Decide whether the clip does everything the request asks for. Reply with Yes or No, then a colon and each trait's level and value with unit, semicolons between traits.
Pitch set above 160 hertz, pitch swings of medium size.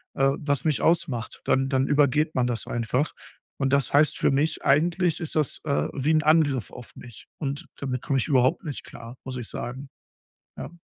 No: medium, 140 Hz; average, 3.1 semitones